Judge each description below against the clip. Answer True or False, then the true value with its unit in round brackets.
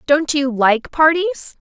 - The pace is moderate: True (145 wpm)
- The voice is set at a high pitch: True (295 Hz)